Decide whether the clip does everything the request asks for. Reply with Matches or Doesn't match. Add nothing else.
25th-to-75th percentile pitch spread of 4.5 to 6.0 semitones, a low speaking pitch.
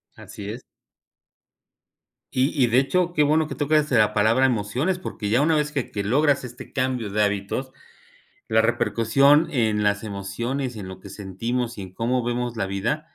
Matches